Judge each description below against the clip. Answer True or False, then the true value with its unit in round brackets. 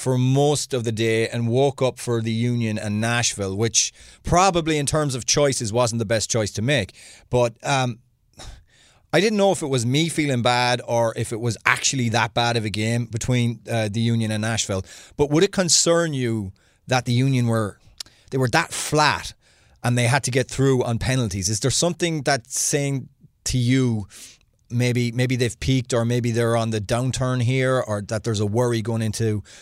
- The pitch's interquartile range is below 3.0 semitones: True (2.6 semitones)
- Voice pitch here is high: False (120 Hz)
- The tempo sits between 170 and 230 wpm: True (200 wpm)